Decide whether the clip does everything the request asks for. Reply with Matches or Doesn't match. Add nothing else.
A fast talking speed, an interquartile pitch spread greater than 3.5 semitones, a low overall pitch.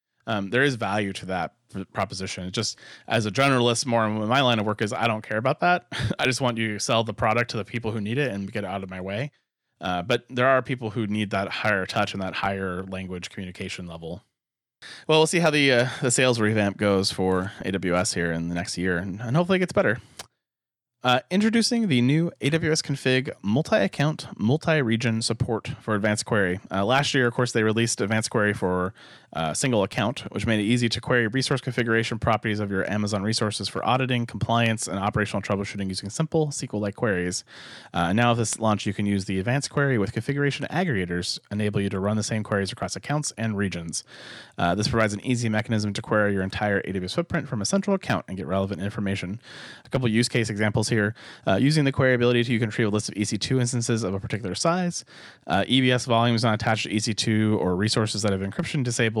Matches